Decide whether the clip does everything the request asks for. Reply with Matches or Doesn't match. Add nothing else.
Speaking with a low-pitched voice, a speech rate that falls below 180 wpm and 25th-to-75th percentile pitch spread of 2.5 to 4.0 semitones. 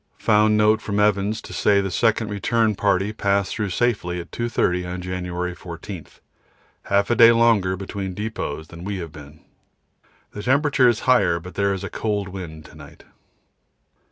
Matches